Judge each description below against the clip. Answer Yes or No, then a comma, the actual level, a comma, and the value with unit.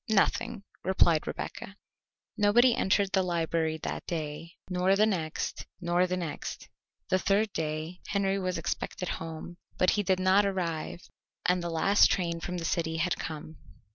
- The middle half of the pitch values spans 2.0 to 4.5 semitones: Yes, average, 2.8 semitones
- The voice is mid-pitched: Yes, medium, 180 Hz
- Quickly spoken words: No, average, 155 wpm